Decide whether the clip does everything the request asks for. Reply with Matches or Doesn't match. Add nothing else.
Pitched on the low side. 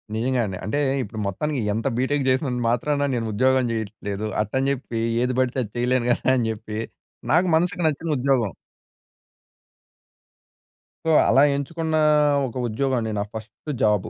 Matches